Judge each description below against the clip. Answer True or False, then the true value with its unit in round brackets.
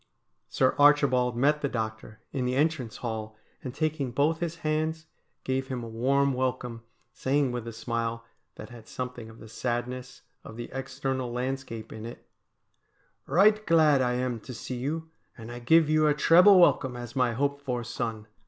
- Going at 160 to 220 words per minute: True (180 wpm)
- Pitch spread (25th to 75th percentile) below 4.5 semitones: True (3.6 semitones)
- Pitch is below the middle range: True (130 Hz)